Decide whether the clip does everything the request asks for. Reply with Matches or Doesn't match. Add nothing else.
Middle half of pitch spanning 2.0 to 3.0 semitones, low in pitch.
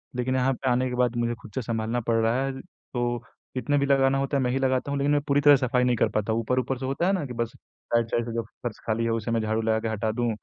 Matches